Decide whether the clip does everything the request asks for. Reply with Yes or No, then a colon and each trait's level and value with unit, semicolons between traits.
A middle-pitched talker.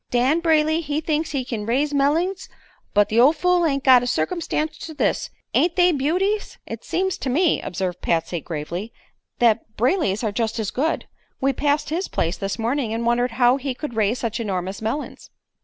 No: very high, 260 Hz